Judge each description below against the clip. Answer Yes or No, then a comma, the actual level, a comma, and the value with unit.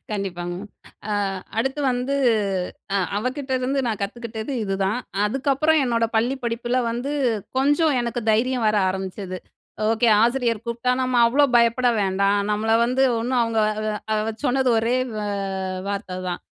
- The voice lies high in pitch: Yes, high, 235 Hz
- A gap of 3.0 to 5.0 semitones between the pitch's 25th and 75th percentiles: Yes, average, 3.5 semitones